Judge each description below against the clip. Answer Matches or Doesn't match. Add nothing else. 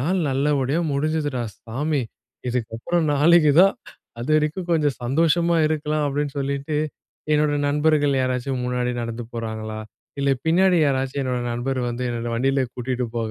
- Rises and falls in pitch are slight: Doesn't match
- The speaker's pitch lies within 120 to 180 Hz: Matches